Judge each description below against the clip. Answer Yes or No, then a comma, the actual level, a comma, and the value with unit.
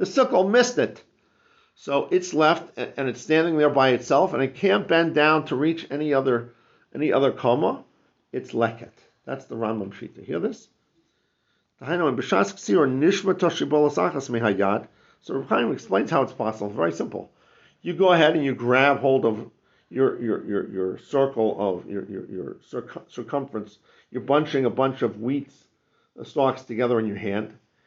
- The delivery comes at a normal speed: Yes, average, 155 wpm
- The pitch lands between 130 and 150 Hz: Yes, low, 135 Hz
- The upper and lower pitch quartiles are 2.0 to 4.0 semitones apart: No, average, 5.1 semitones